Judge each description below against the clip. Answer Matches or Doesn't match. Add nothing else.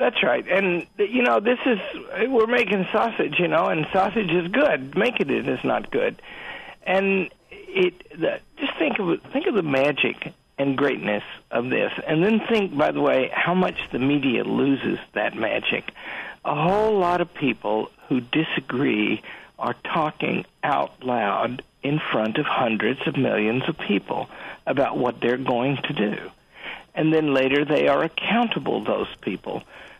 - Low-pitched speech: Doesn't match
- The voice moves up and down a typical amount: Doesn't match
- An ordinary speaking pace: Matches